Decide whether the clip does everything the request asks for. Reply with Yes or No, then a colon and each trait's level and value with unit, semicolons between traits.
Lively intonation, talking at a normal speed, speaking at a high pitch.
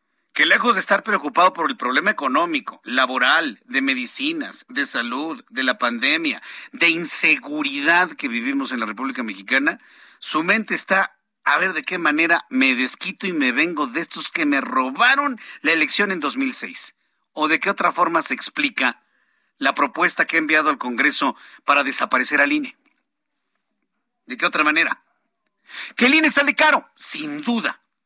Yes: wide, 6.5 semitones; average, 165 wpm; very high, 270 Hz